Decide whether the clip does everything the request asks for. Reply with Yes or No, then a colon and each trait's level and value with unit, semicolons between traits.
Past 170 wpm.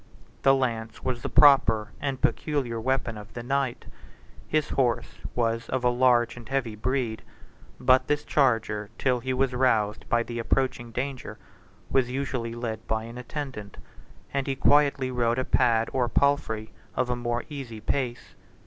No: average, 160 wpm